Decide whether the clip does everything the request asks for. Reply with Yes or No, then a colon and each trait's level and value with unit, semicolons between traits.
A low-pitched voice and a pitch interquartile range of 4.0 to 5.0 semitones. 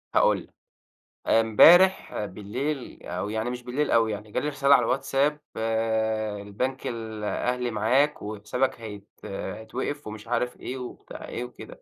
No: low, 115 Hz; average, 3.4 semitones